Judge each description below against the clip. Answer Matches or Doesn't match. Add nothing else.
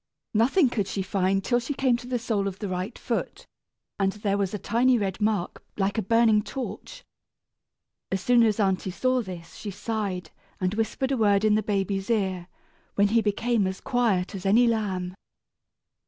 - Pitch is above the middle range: Matches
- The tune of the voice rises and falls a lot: Doesn't match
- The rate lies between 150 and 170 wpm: Doesn't match